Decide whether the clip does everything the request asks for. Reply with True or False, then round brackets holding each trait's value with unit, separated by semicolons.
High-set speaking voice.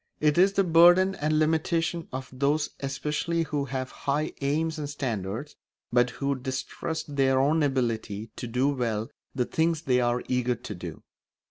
False (140 Hz)